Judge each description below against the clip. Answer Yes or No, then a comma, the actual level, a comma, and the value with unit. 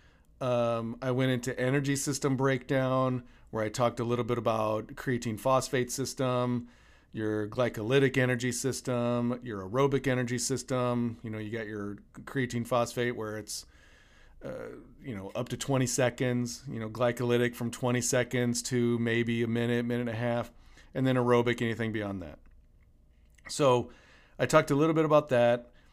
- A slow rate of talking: No, average, 160 wpm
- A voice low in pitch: Yes, low, 120 Hz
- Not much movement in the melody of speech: Yes, narrow, 1.9 semitones